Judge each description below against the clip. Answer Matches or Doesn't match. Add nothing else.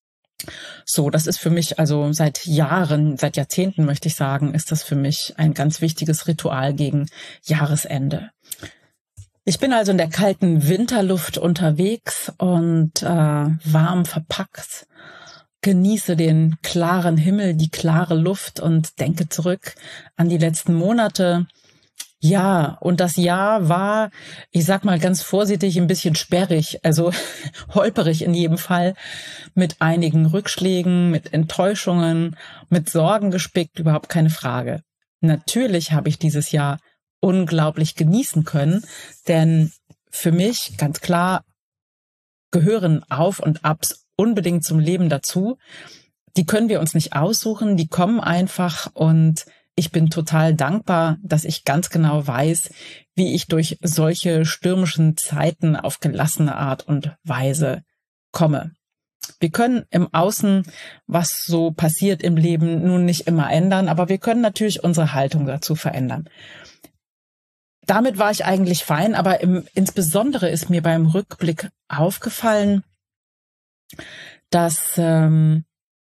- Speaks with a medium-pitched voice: Matches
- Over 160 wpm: Doesn't match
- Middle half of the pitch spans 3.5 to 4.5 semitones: Doesn't match